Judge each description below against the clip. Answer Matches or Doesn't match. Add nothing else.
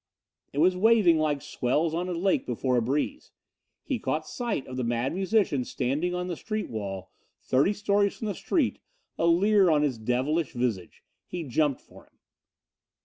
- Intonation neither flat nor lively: Doesn't match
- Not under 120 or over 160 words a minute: Doesn't match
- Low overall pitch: Doesn't match